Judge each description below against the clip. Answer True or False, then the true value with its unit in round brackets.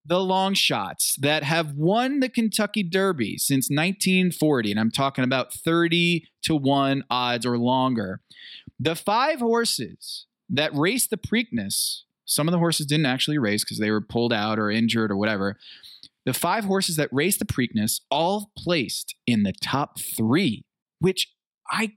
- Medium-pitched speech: True (155 Hz)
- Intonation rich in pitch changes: True (7.6 semitones)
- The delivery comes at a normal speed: True (160 wpm)